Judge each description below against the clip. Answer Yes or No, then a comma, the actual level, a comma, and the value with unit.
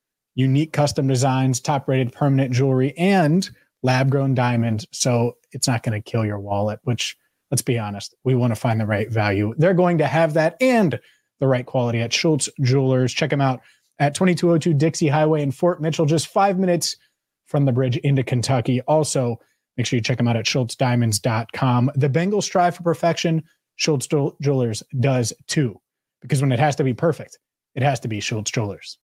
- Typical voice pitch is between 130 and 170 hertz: Yes, low, 135 Hz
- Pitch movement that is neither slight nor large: Yes, average, 4.3 semitones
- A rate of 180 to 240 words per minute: Yes, average, 190 wpm